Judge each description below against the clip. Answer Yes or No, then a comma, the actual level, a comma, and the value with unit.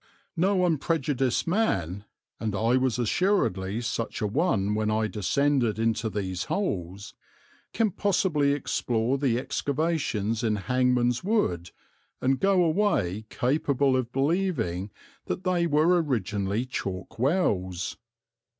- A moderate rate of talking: No, slow, 115 wpm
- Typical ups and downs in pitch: No, wide, 7.5 semitones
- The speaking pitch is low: Yes, low, 125 Hz